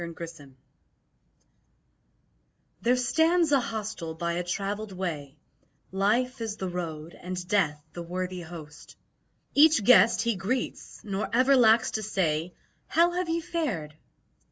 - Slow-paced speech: Yes, slow, 130 wpm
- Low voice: No, high, 195 Hz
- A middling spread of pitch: No, wide, 6.4 semitones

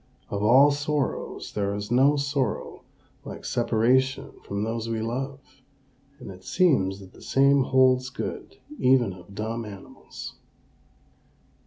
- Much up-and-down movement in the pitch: No, average, 4.4 semitones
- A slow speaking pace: Yes, slow, 130 wpm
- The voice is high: No, low, 125 Hz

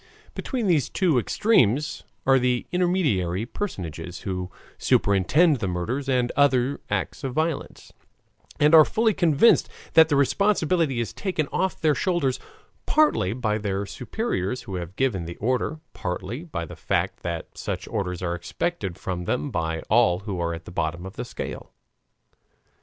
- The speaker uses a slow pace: No, average, 155 wpm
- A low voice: Yes, low, 125 Hz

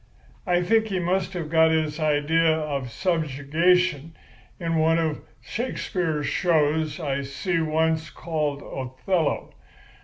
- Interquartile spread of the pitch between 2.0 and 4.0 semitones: Yes, average, 2.7 semitones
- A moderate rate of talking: No, slow, 120 wpm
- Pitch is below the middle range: No, medium, 160 Hz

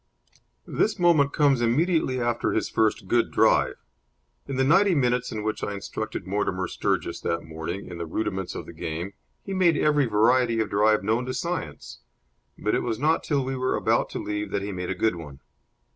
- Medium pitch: No, low, 115 Hz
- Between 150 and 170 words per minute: No, average, 195 wpm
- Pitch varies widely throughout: Yes, wide, 6.0 semitones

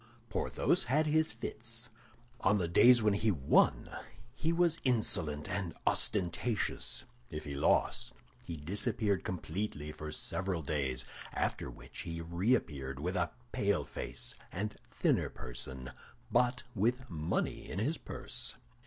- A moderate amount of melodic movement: No, wide, 7.1 semitones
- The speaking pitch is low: Yes, very low, 95 Hz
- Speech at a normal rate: No, slow, 130 wpm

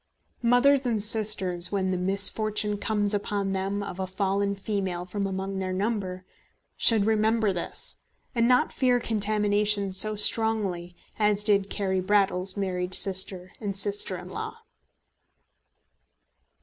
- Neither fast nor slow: No, slow, 130 wpm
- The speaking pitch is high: Yes, high, 200 Hz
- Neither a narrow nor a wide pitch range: No, narrow, 2.1 semitones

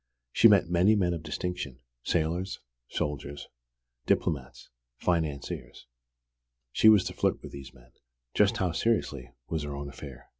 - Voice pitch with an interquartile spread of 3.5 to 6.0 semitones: Yes, average, 4.2 semitones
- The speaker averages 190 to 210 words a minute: No, average, 140 wpm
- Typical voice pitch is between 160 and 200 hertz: No, very low, 80 Hz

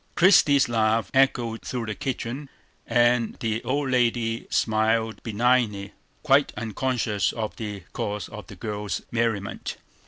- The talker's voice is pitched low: Yes, low, 115 Hz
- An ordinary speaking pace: No, slow, 125 wpm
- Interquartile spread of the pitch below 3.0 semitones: Yes, narrow, 2.6 semitones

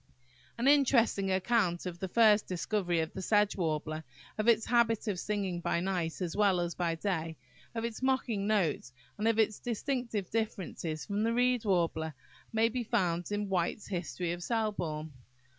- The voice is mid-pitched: No, high, 200 Hz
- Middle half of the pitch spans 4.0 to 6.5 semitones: Yes, average, 4.6 semitones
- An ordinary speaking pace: Yes, average, 170 wpm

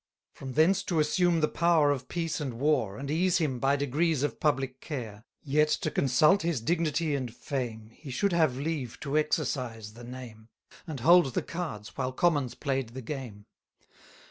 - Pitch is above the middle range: No, medium, 140 Hz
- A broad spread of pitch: No, average, 4.1 semitones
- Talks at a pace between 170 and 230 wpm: Yes, average, 180 wpm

